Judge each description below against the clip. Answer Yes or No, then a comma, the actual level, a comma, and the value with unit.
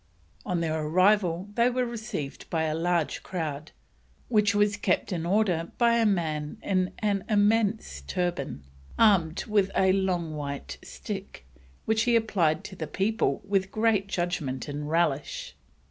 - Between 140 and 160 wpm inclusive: Yes, average, 145 wpm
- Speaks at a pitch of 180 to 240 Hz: Yes, medium, 185 Hz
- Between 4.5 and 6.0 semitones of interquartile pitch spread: Yes, average, 4.8 semitones